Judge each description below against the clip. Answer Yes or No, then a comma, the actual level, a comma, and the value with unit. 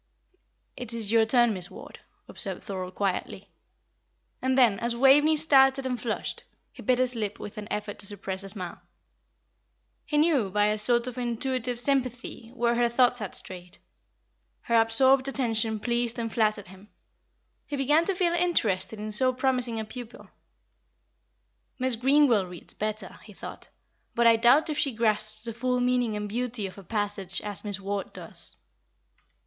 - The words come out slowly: No, average, 165 wpm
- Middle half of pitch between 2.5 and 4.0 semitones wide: Yes, average, 3.5 semitones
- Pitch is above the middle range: Yes, high, 230 Hz